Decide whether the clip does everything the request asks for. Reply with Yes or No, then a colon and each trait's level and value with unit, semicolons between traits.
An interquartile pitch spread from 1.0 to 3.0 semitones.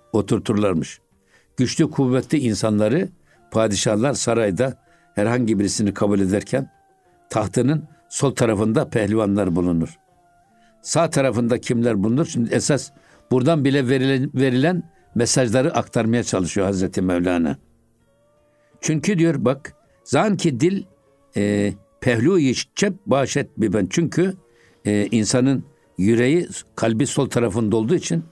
No: wide, 5.4 semitones